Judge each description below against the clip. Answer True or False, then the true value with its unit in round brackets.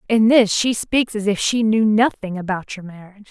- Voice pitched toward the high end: True (210 Hz)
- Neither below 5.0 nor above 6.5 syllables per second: True (5.1 syllables/s)